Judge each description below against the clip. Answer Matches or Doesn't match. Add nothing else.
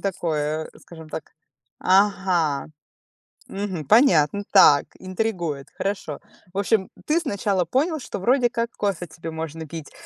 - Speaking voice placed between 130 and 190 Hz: Matches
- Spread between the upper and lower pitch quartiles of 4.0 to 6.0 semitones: Matches